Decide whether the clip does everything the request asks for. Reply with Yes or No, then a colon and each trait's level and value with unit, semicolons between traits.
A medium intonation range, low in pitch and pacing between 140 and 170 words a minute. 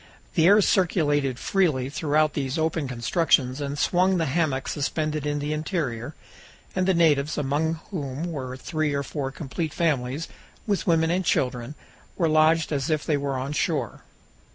No: average, 3.0 semitones; medium, 150 Hz; average, 160 wpm